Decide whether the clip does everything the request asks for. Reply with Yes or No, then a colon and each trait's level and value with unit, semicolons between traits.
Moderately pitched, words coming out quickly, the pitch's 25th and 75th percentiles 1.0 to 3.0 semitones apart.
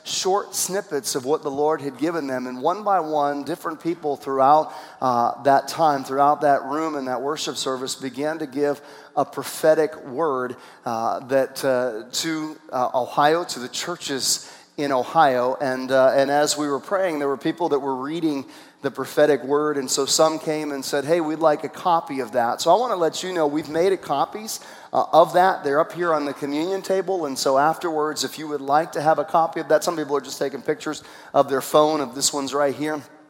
Yes: medium, 150 Hz; fast, 215 wpm; narrow, 2.5 semitones